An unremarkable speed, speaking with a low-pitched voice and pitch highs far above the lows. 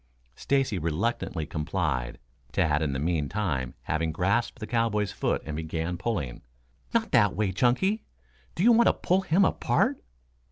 Yes: average, 150 wpm; very low, 90 Hz; wide, 7.3 semitones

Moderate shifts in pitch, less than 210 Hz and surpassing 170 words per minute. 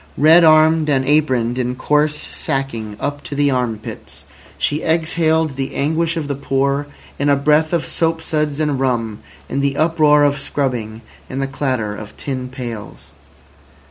No: average, 3.1 semitones; medium, 140 Hz; average, 165 wpm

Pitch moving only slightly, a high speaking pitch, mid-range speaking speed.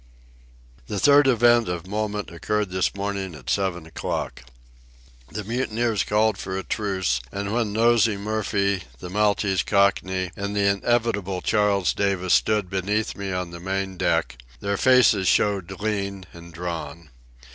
No: narrow, 2.3 semitones; low, 100 Hz; average, 145 wpm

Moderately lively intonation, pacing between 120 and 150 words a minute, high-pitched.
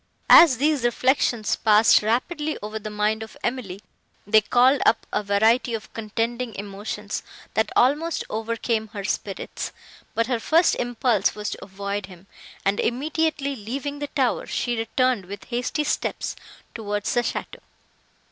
Yes: average, 3.6 semitones; average, 145 wpm; high, 225 Hz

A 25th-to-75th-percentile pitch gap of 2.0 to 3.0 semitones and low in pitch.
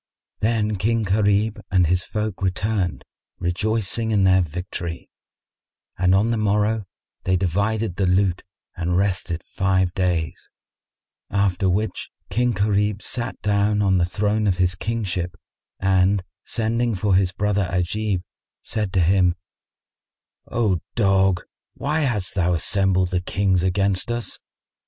Yes: average, 2.7 semitones; very low, 95 Hz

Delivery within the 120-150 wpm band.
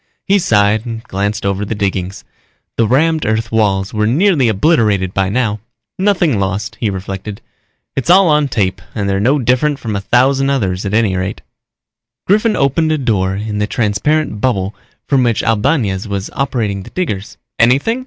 No: average, 175 wpm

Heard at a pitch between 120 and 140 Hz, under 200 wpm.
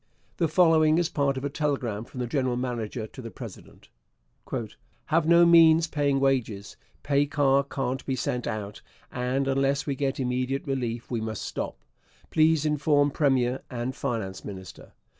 Yes: low, 135 Hz; average, 160 wpm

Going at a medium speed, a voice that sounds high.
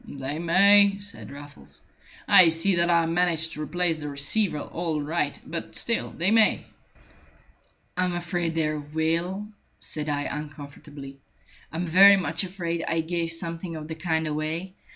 No: average, 150 wpm; medium, 165 Hz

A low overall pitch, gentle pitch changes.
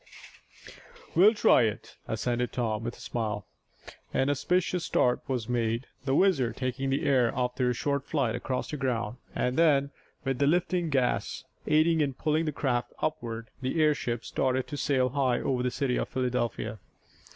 No: low, 130 Hz; average, 3.0 semitones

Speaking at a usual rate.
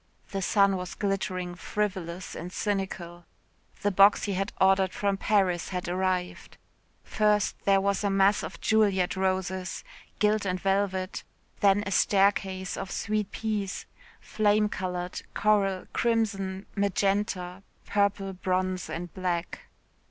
No: slow, 125 wpm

